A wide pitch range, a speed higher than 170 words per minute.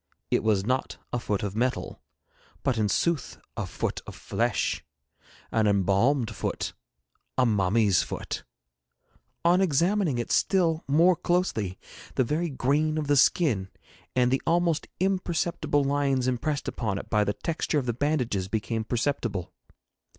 No: wide, 6.3 semitones; average, 145 wpm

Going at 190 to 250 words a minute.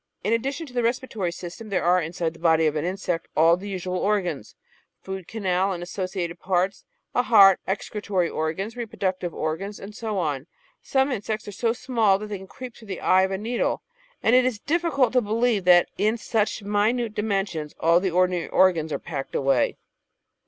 Yes: average, 195 wpm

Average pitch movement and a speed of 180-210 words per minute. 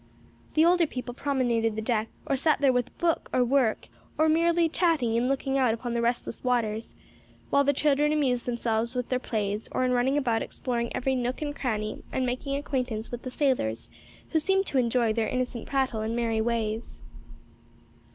Yes: average, 3.3 semitones; average, 185 wpm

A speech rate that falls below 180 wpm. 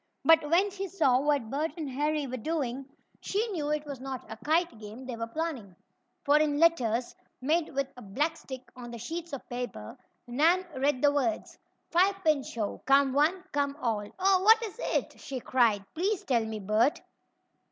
No: average, 185 wpm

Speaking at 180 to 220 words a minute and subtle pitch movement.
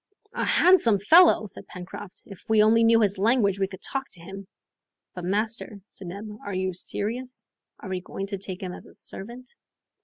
No: average, 190 wpm; average, 3.2 semitones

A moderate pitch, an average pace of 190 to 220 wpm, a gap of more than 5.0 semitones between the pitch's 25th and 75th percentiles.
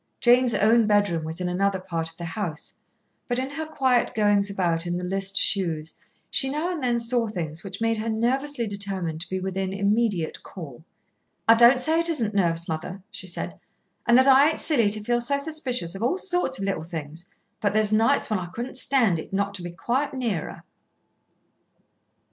No: high, 205 Hz; average, 200 wpm; wide, 5.5 semitones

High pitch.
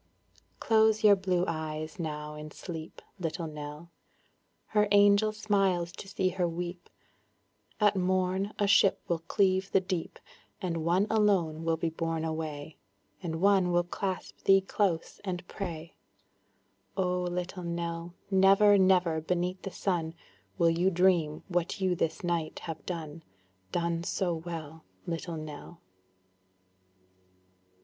No: medium, 175 Hz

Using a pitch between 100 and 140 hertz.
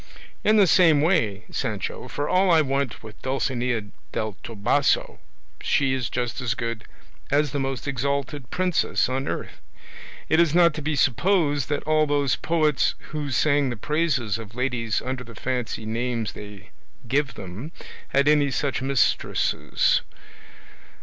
Yes: low, 135 Hz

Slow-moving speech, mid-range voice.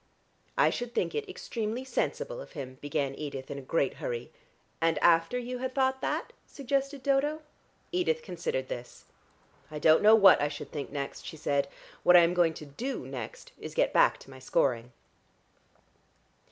No: average, 175 wpm; medium, 175 Hz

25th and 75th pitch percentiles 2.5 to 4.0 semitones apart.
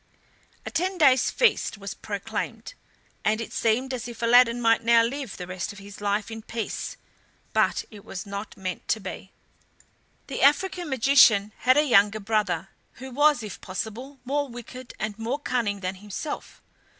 No: average, 4.4 semitones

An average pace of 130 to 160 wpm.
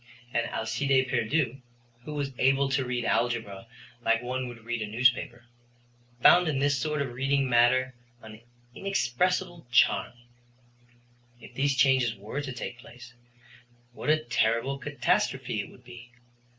Yes: average, 140 wpm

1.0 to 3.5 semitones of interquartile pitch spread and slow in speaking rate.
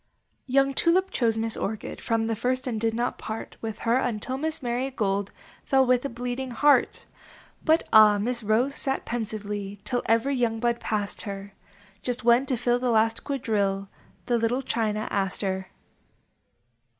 No: average, 3.0 semitones; average, 160 wpm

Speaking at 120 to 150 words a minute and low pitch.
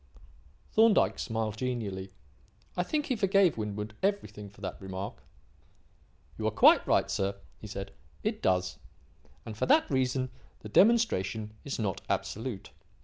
Yes: average, 140 wpm; low, 110 Hz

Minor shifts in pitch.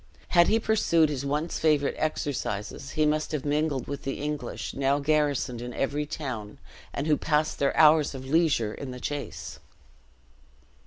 Yes: narrow, 2.2 semitones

